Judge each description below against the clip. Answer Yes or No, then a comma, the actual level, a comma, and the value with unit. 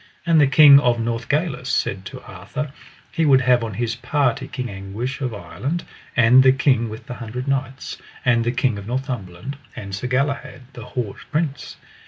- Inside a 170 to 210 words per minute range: Yes, average, 180 wpm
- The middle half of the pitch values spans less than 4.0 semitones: Yes, average, 3.1 semitones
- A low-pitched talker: Yes, low, 125 Hz